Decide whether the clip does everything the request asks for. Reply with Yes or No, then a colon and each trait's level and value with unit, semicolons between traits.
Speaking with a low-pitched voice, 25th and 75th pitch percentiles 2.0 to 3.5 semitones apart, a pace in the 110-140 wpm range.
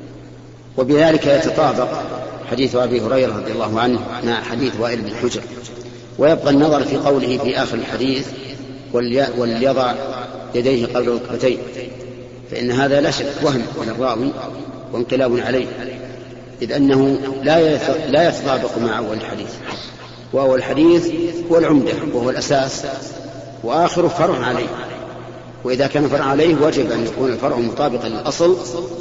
Yes: low, 130 Hz; narrow, 2.4 semitones; average, 120 wpm